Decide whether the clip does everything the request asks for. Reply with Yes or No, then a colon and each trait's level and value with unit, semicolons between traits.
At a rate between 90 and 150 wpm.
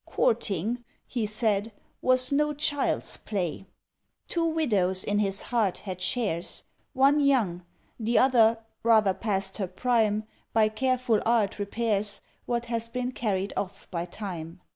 Yes: slow, 135 wpm